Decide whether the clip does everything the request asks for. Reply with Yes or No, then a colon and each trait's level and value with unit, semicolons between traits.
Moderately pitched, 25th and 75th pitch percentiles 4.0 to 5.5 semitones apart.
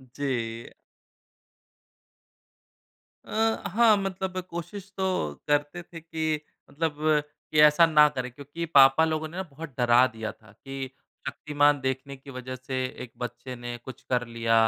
Yes: medium, 145 Hz; average, 4.5 semitones